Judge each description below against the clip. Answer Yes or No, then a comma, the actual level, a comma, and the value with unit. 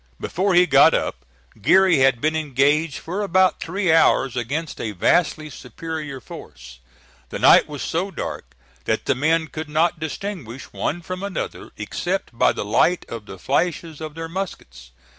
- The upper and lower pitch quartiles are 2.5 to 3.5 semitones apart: No, average, 4.8 semitones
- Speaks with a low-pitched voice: No, medium, 160 Hz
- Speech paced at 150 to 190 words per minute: Yes, average, 160 wpm